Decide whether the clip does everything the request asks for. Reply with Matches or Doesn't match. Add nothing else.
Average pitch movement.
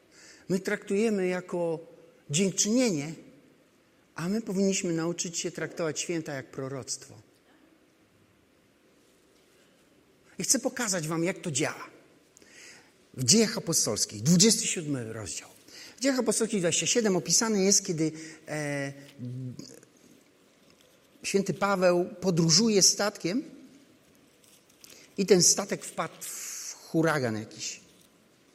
Matches